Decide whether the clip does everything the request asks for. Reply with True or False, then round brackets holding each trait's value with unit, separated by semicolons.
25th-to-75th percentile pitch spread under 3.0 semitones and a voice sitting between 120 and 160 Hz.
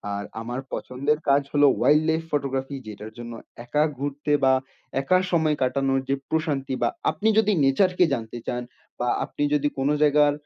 True (2.4 semitones; 140 Hz)